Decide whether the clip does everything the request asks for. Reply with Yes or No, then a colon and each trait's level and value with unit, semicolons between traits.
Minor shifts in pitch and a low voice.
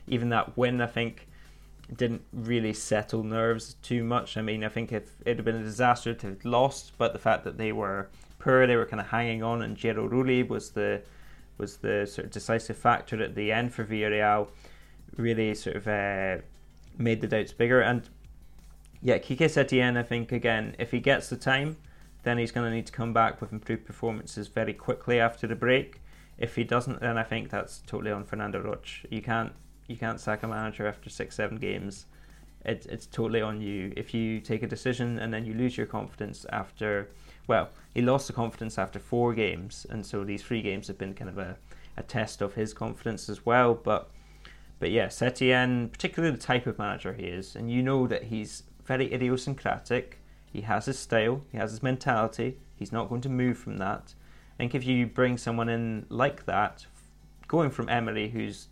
Yes: narrow, 2.3 semitones; low, 115 Hz